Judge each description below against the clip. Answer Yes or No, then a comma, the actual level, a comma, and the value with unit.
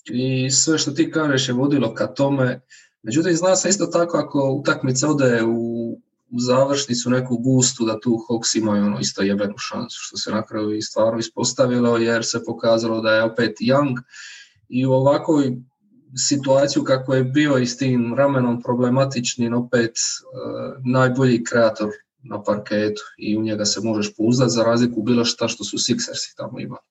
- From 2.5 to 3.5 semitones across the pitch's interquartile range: Yes, average, 3.0 semitones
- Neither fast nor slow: Yes, average, 170 wpm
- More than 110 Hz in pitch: Yes, low, 125 Hz